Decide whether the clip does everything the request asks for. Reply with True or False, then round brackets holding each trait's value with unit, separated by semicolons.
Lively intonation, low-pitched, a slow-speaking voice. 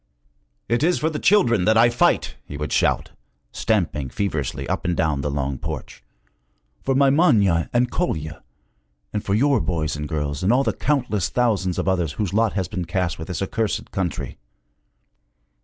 False (7.1 semitones; 95 Hz; 175 wpm)